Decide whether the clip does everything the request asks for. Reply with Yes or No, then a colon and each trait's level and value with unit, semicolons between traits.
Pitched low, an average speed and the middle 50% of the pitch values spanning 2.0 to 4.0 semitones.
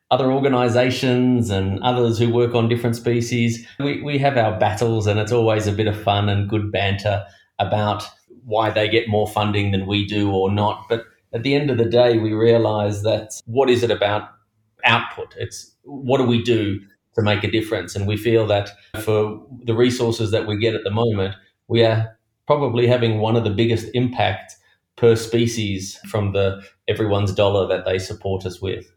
Yes: low, 110 Hz; average, 190 wpm; narrow, 2.4 semitones